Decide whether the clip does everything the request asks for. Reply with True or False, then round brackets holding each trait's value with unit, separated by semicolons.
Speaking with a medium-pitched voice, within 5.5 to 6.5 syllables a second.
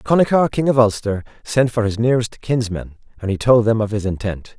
False (115 Hz; 5.6 syllables/s)